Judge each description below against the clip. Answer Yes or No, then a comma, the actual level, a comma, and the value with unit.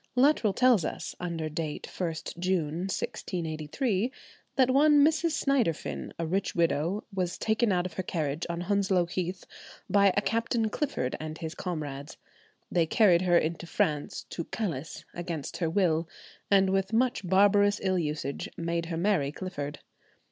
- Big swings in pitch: No, average, 3.9 semitones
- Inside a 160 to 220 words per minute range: No, average, 150 wpm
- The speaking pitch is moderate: Yes, medium, 180 Hz